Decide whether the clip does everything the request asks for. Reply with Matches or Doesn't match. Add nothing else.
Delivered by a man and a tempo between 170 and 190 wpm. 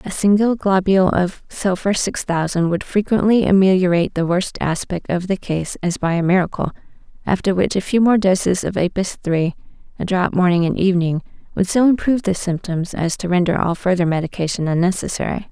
Doesn't match